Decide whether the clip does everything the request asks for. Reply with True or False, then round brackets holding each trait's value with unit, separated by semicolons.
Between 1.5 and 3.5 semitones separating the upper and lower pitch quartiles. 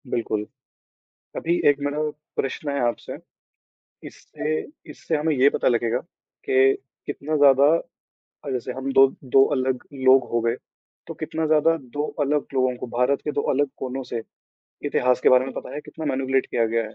True (2.5 semitones)